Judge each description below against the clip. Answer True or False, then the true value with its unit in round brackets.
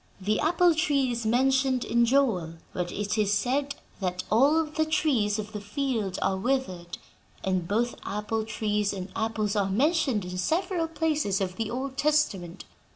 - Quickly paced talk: False (160 wpm)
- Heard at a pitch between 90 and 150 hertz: False (225 Hz)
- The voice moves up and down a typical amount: False (5.7 semitones)